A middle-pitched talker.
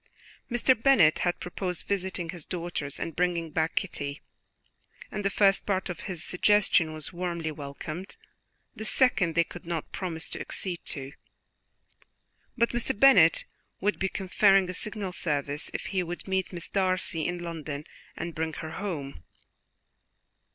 Yes: medium, 175 Hz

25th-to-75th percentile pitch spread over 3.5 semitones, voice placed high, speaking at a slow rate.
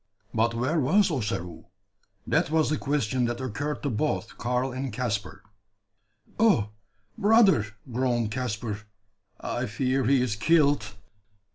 No: average, 4.6 semitones; low, 125 Hz; slow, 125 wpm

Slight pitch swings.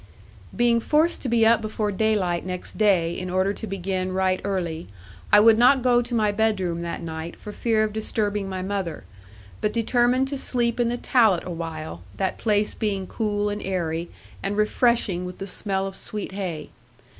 No: average, 3.4 semitones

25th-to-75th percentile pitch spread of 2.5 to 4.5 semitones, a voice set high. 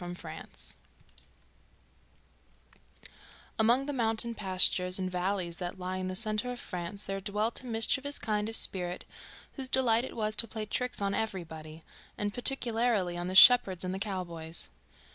Yes: average, 4.0 semitones; high, 205 Hz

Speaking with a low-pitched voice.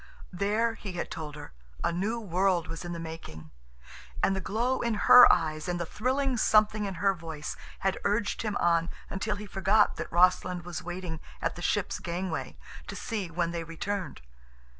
No: medium, 185 Hz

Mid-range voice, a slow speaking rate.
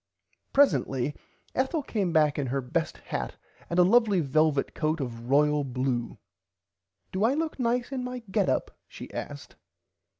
No: medium, 160 Hz; average, 155 wpm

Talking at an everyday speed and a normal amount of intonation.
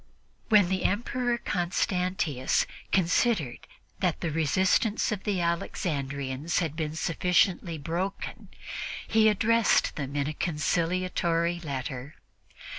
No: slow, 105 wpm; average, 4.0 semitones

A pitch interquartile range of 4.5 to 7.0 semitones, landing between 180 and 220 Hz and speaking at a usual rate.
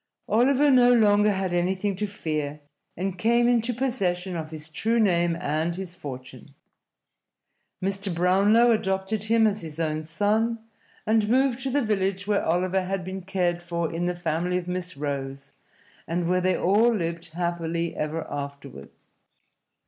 No: average, 4.1 semitones; medium, 185 Hz; average, 155 wpm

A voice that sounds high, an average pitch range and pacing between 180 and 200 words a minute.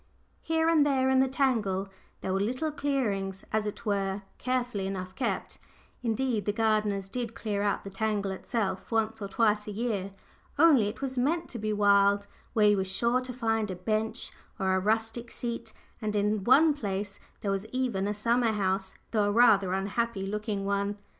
Yes: high, 215 Hz; average, 3.4 semitones; average, 185 wpm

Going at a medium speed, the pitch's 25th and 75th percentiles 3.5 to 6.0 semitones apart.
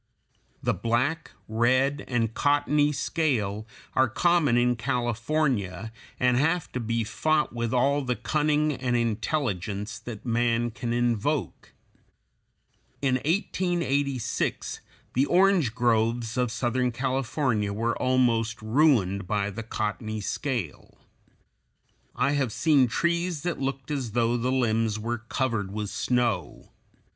No: slow, 120 wpm; average, 3.9 semitones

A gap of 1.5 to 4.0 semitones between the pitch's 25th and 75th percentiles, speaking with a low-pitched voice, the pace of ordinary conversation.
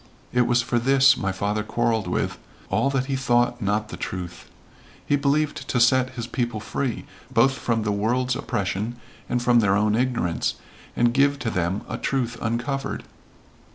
Yes: average, 3.4 semitones; low, 120 Hz; average, 170 wpm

